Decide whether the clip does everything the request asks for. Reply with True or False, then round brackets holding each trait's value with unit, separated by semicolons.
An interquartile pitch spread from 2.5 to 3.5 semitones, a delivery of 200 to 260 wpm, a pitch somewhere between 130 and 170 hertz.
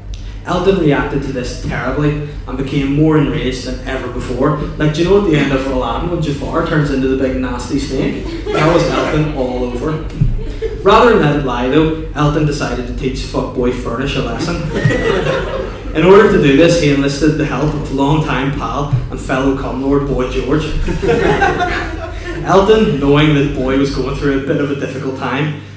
False (2.8 semitones; 180 wpm; 140 Hz)